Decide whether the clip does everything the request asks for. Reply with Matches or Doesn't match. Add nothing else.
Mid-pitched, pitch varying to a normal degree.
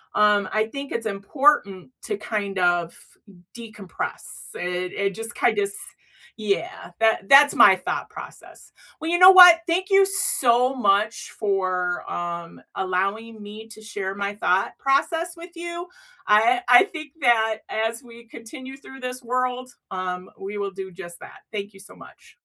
Doesn't match